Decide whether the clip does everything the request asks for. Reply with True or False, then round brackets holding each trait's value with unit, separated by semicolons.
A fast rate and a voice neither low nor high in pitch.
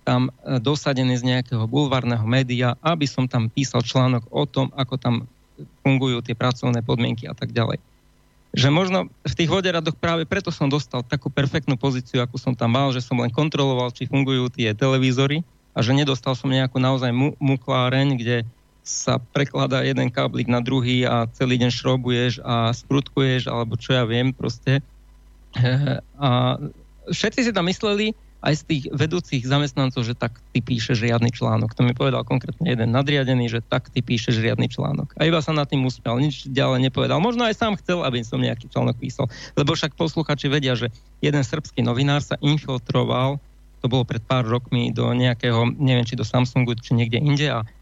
False (180 wpm; 130 Hz)